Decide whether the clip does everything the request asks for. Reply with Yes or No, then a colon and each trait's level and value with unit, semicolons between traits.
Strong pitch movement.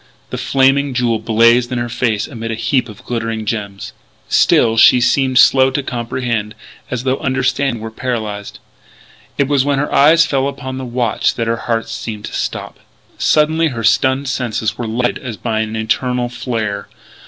No: average, 2.7 semitones